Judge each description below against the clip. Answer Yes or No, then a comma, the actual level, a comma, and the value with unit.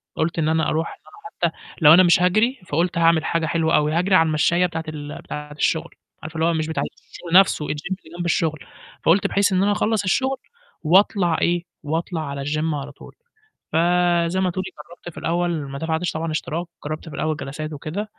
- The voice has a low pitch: No, medium, 165 Hz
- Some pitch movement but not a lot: No, narrow, 2.3 semitones